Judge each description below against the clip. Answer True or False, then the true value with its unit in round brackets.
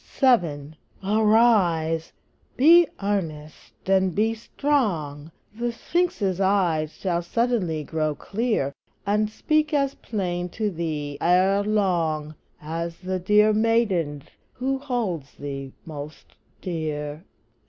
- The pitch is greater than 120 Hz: True (185 Hz)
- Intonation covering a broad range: True (5.9 semitones)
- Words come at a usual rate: False (105 wpm)